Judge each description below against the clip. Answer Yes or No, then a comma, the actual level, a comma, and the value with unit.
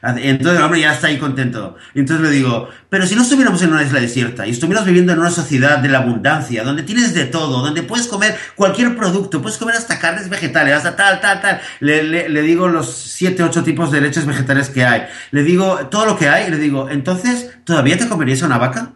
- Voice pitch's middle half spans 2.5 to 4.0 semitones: No, average, 5.2 semitones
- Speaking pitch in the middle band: Yes, medium, 160 Hz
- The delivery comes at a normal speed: No, fast, 230 wpm